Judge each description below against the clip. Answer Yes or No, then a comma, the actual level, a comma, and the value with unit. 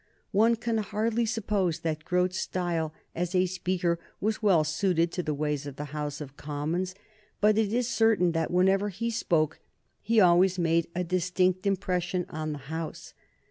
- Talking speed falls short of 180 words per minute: Yes, average, 170 wpm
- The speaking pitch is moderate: Yes, medium, 180 Hz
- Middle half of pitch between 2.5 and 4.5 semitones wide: Yes, average, 3.9 semitones